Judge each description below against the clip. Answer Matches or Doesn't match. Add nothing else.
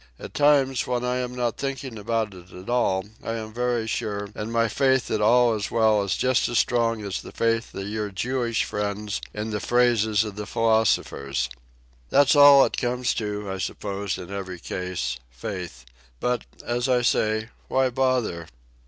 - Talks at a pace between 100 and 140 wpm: Doesn't match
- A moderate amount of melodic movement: Matches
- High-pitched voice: Doesn't match